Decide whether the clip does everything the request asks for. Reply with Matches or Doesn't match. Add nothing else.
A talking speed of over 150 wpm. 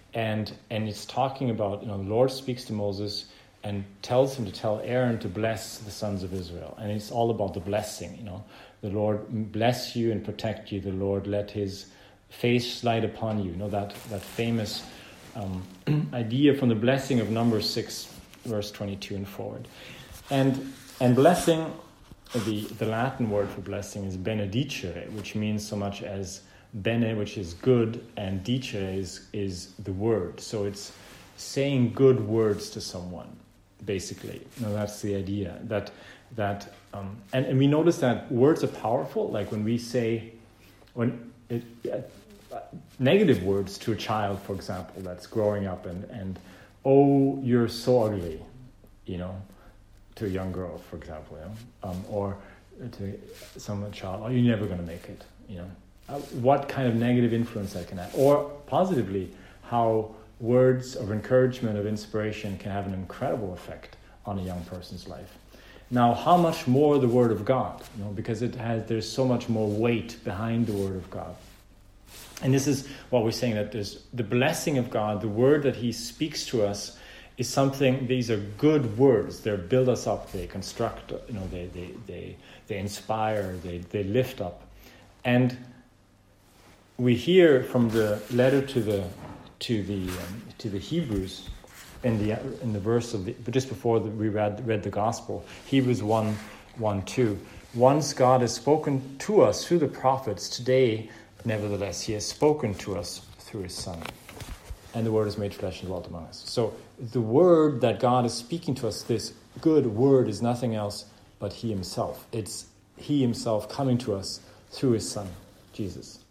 Matches